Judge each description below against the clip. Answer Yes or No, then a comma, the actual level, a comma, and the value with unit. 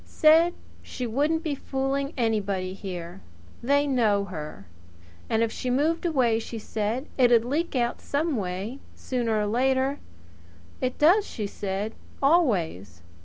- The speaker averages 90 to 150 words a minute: Yes, slow, 135 wpm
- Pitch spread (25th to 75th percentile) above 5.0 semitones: Yes, wide, 5.4 semitones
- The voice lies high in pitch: Yes, high, 240 Hz